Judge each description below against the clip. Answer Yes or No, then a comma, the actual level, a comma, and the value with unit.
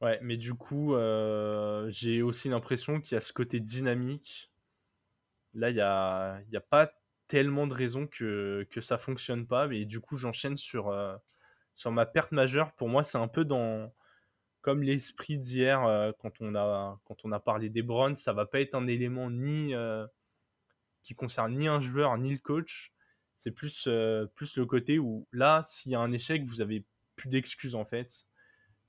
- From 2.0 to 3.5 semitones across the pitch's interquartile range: No, average, 3.9 semitones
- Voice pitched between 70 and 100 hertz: No, low, 120 Hz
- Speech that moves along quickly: No, average, 190 wpm